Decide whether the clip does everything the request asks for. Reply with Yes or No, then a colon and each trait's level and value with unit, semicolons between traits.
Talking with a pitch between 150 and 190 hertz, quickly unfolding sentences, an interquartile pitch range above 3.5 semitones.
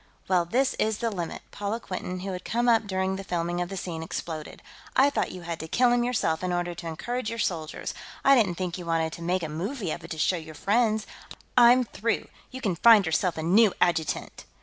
Yes: medium, 185 Hz; fast, 230 wpm; average, 5.1 semitones